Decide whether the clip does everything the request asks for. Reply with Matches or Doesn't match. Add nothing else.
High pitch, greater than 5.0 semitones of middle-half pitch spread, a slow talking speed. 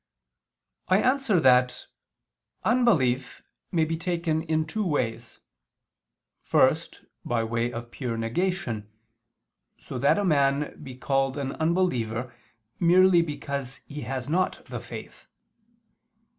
Doesn't match